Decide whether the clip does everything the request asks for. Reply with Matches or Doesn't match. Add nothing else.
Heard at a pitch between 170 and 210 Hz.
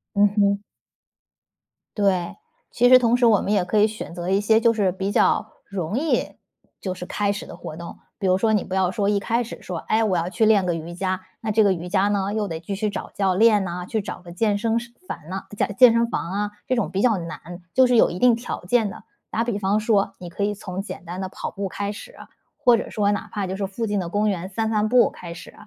Matches